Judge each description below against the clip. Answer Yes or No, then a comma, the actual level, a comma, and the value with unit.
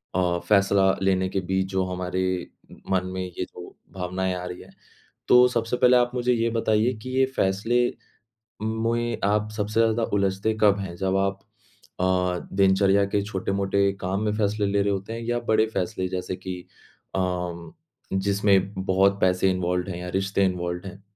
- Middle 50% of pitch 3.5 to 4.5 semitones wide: No, narrow, 2.5 semitones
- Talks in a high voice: No, very low, 95 Hz